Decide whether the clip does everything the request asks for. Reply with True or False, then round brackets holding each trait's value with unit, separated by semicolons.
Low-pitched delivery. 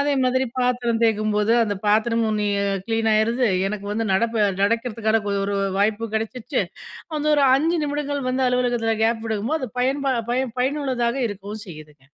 False (230 Hz)